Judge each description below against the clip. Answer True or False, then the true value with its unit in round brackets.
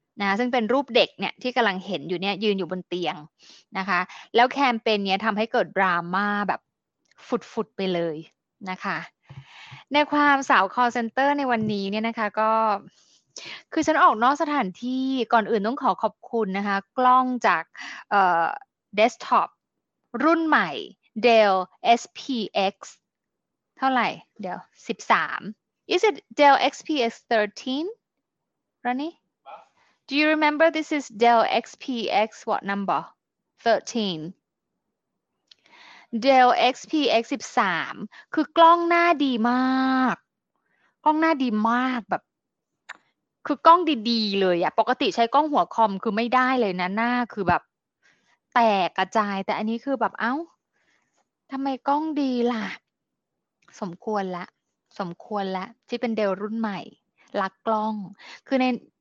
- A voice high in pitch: True (235 Hz)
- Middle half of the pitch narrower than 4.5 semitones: False (5.1 semitones)